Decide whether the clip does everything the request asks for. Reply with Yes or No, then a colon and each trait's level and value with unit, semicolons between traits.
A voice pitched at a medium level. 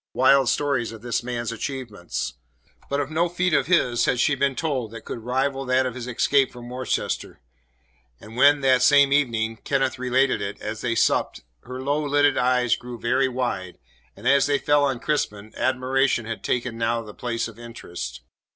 No: low, 125 Hz